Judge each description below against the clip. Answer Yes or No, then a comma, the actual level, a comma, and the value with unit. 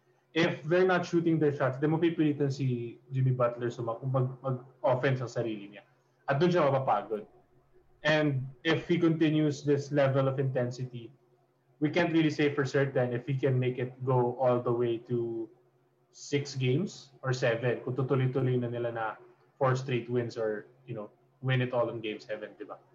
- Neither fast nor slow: Yes, average, 180 wpm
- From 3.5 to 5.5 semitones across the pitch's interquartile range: No, average, 2.9 semitones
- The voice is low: Yes, low, 130 Hz